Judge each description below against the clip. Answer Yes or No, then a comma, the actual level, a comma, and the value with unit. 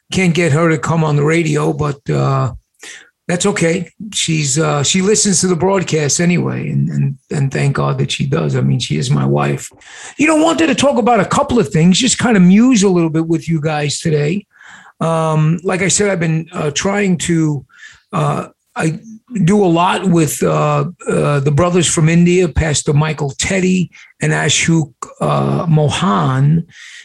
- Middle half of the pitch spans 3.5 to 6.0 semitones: Yes, average, 4.2 semitones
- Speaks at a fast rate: No, average, 185 wpm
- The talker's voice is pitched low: No, medium, 165 Hz